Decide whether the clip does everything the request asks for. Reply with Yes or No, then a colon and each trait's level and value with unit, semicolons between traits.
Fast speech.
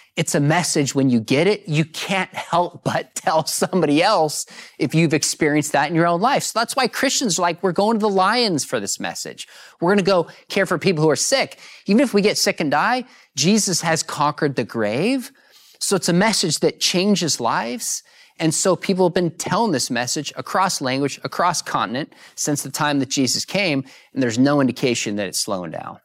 Yes: fast, 210 wpm